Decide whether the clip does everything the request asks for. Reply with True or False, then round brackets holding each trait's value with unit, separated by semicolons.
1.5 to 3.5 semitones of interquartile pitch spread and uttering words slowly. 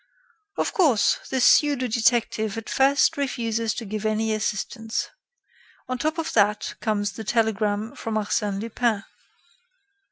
True (2.6 semitones; 130 wpm)